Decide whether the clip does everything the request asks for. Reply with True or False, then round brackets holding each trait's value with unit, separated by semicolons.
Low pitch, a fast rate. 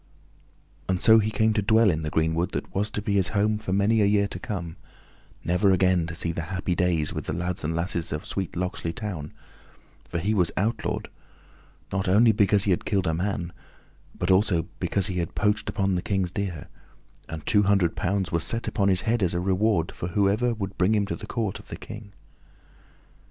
True (95 Hz; 210 wpm)